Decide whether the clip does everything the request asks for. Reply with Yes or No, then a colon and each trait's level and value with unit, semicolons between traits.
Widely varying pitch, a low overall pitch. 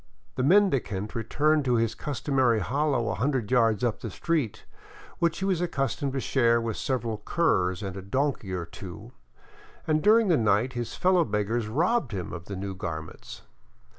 Yes: wide, 6.1 semitones; low, 120 Hz